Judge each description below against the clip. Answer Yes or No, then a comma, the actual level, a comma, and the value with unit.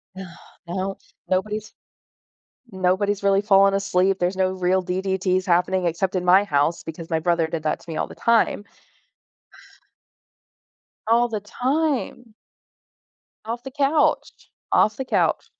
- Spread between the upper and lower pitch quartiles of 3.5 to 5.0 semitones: No, average, 2.9 semitones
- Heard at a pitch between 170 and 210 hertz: Yes, high, 190 Hz